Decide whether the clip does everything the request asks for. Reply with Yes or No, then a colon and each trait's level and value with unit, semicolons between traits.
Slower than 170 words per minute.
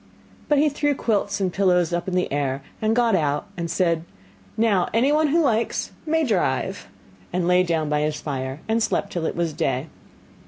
No: average, 185 wpm